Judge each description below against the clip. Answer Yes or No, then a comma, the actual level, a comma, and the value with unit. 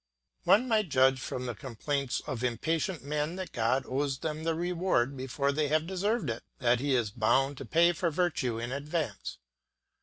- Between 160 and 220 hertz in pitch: No, medium, 140 Hz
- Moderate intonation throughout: Yes, average, 4.6 semitones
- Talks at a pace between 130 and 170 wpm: No, average, 180 wpm